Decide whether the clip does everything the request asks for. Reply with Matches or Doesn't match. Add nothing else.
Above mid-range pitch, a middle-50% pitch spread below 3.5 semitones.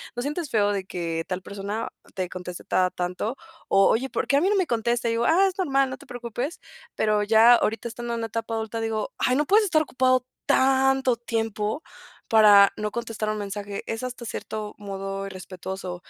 Doesn't match